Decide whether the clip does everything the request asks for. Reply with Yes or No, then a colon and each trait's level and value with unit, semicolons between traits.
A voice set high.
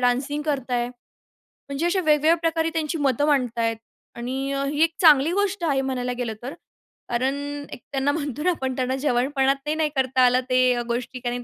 Yes: very high, 270 Hz